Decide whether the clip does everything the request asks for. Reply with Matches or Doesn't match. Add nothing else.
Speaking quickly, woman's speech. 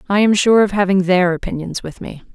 Matches